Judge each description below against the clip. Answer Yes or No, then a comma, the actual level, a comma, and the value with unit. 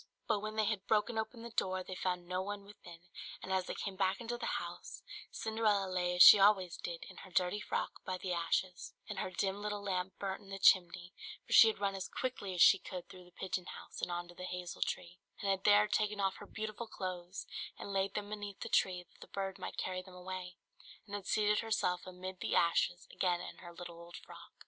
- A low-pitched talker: No, high, 190 Hz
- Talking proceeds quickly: Yes, fast, 235 wpm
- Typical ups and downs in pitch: No, narrow, 2.3 semitones